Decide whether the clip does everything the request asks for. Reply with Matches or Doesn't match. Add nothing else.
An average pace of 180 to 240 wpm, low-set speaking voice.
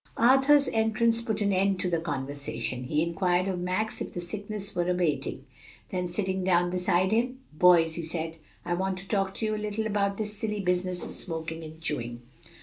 Doesn't match